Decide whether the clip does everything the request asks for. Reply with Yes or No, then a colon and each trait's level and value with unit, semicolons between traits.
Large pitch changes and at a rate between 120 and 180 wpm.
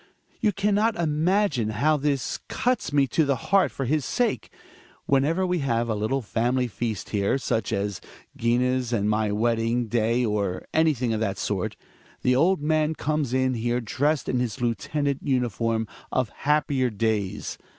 No: average, 4.8 semitones; average, 170 wpm